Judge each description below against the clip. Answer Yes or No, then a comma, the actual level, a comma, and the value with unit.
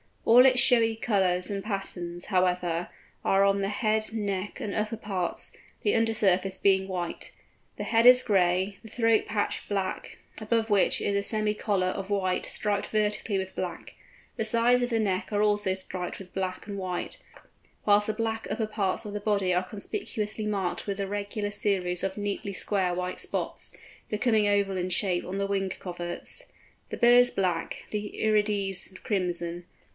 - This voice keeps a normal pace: Yes, average, 175 wpm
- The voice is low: No, high, 200 Hz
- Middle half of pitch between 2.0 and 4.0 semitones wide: Yes, narrow, 2.4 semitones